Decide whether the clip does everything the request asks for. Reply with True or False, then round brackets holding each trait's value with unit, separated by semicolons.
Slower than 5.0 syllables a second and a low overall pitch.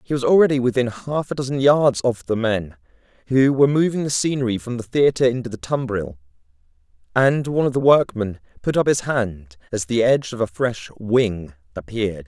False (5.4 syllables/s; 120 Hz)